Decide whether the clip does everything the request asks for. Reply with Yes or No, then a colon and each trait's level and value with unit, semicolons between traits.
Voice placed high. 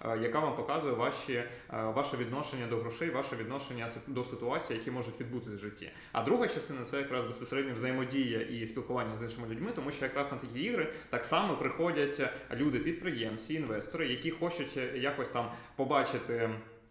No: low, 125 Hz